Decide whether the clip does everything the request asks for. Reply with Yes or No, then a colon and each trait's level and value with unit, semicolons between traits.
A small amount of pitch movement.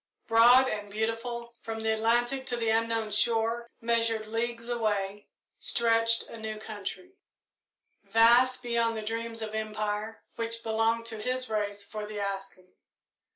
Yes: narrow, 1.4 semitones